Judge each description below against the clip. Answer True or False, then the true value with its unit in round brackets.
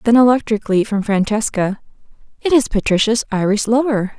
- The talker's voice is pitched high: True (220 Hz)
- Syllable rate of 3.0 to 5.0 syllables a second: False (5.6 syllables/s)